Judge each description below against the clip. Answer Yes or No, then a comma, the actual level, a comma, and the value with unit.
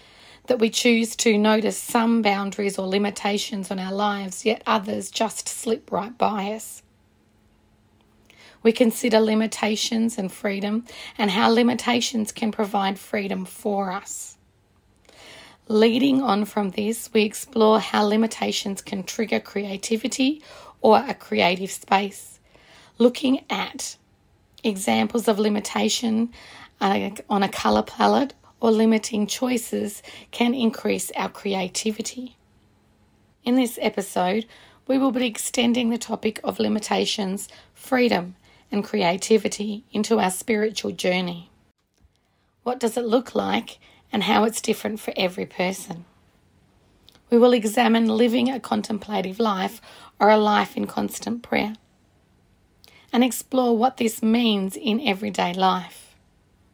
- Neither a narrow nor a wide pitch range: Yes, average, 3.3 semitones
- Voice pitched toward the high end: Yes, high, 215 Hz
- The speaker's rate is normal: No, slow, 120 wpm